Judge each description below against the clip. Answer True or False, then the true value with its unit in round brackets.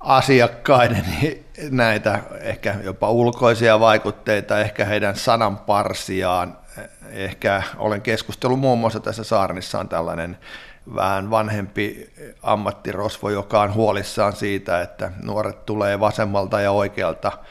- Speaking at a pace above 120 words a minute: False (105 wpm)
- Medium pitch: False (105 Hz)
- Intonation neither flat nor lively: False (1.9 semitones)